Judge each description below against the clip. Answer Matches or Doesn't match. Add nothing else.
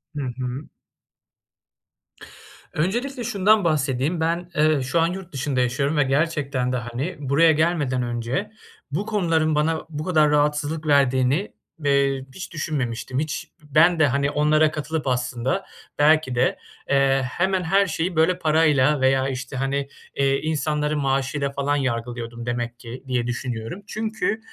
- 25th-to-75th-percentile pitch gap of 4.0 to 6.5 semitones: Doesn't match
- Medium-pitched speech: Matches